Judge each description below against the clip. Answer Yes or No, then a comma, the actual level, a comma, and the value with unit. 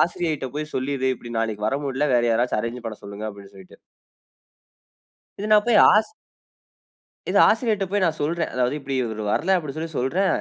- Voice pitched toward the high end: No, low, 135 Hz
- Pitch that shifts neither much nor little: No, wide, 6.8 semitones